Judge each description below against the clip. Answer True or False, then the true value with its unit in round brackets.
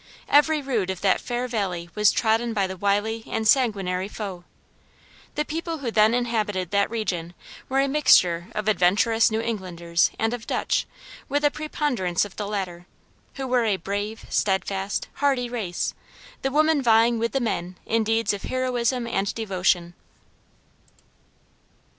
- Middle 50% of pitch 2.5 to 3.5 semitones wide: False (4.4 semitones)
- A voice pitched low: False (220 Hz)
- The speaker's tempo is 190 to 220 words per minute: False (155 wpm)